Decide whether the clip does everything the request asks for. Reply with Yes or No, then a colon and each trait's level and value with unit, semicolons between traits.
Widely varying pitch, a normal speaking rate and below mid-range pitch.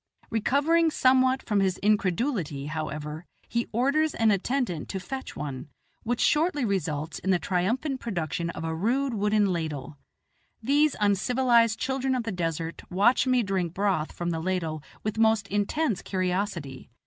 No: wide, 6.7 semitones; average, 150 wpm; high, 205 Hz